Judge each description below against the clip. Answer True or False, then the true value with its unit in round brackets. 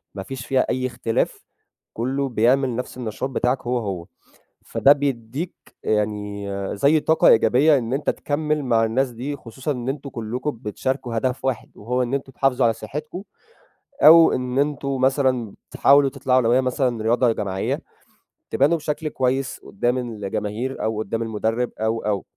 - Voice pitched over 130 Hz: False (125 Hz)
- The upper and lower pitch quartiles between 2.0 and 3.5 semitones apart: True (3.2 semitones)